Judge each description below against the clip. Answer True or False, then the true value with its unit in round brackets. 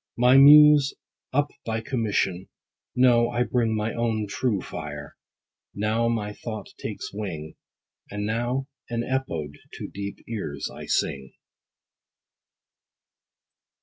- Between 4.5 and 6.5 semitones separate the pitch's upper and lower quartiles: False (3.7 semitones)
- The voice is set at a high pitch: False (110 Hz)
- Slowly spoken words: True (115 wpm)